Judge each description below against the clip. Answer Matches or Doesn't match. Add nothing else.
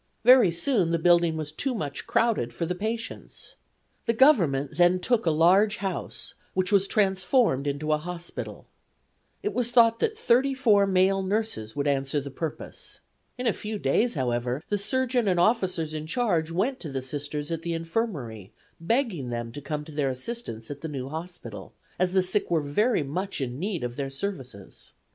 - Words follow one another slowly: Doesn't match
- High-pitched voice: Doesn't match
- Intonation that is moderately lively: Doesn't match